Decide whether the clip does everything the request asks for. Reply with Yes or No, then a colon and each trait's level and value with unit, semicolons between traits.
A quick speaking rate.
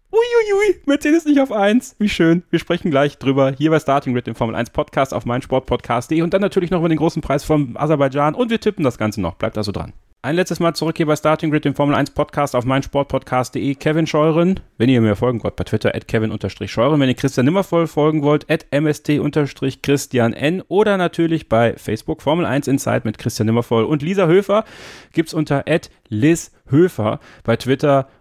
Yes: fast, 195 wpm